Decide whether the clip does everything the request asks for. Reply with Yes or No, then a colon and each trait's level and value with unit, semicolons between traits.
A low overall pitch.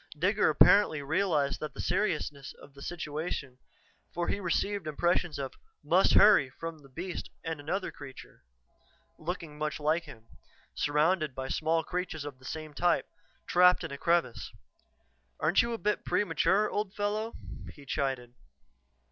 No: medium, 160 Hz